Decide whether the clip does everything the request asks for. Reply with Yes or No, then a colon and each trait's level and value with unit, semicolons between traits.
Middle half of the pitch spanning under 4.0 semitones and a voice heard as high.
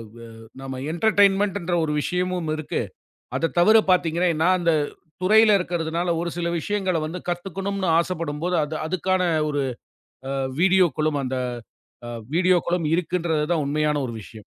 No: average, 2.9 semitones; medium, 175 Hz